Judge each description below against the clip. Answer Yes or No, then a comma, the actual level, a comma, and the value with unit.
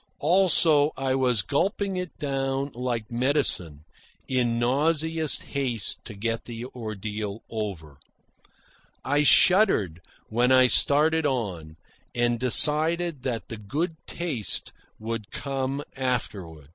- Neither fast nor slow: No, slow, 110 wpm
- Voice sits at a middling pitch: No, low, 130 Hz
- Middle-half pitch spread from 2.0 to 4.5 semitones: No, average, 5.1 semitones